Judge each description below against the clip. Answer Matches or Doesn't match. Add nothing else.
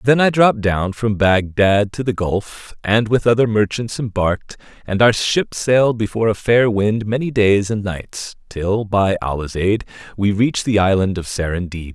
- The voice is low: Matches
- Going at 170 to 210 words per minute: Matches